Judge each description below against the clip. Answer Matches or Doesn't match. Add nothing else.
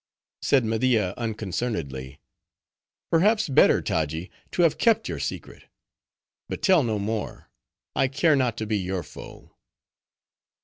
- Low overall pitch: Matches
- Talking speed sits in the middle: Doesn't match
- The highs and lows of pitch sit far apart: Matches